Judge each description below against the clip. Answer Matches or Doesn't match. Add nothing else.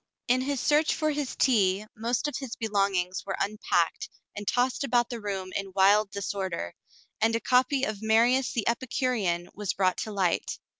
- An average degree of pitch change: Matches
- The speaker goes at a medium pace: Matches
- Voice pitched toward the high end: Matches